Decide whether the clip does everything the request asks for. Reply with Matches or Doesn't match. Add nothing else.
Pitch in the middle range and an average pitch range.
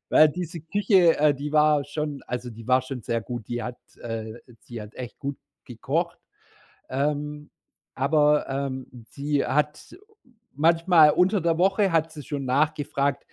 Matches